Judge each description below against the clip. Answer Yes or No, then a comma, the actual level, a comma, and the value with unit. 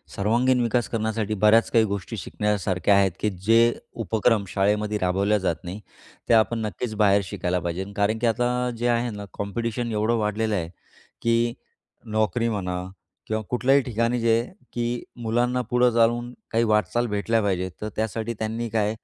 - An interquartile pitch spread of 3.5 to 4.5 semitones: No, narrow, 2.4 semitones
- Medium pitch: No, low, 110 Hz